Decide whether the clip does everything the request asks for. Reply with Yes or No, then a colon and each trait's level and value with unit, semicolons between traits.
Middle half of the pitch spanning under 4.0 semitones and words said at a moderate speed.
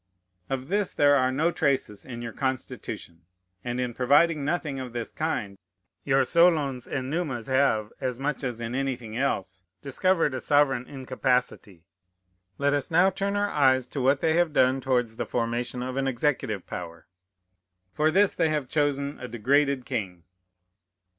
Yes: average, 3.2 semitones; average, 160 wpm